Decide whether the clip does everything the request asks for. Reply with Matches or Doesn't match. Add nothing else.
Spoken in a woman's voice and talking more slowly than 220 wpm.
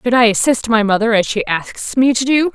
Doesn't match